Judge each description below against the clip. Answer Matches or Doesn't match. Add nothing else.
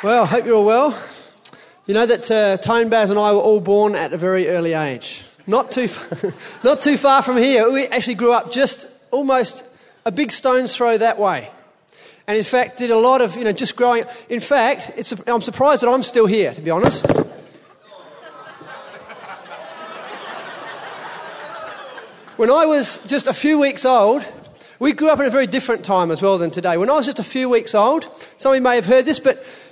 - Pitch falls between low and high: Doesn't match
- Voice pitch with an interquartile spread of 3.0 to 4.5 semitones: Matches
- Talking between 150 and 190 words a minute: Doesn't match